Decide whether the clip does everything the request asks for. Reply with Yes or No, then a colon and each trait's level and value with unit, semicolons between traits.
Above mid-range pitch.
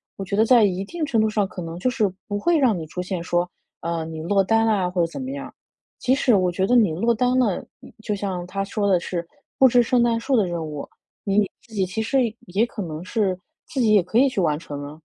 Yes: high, 200 Hz